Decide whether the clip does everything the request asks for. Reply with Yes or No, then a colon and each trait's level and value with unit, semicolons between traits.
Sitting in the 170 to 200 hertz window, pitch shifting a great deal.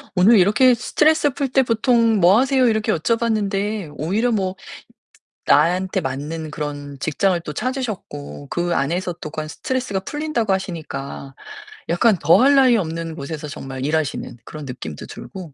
Yes: medium, 185 Hz; wide, 7.1 semitones